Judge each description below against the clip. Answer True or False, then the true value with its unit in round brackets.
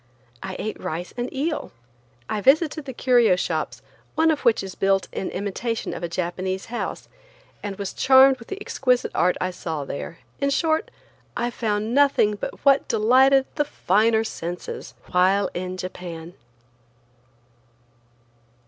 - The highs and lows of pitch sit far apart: True (6.3 semitones)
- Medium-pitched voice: False (215 Hz)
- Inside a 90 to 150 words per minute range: True (145 wpm)